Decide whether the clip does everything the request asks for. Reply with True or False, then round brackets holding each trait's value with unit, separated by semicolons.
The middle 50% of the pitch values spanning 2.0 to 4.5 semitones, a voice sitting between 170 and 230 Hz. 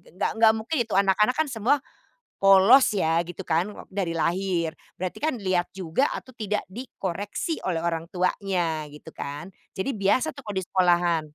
True (4.1 semitones; 190 Hz)